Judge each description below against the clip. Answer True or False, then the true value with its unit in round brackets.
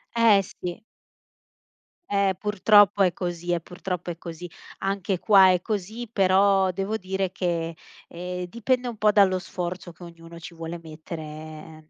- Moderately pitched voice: True (180 Hz)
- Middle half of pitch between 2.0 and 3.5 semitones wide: True (2.7 semitones)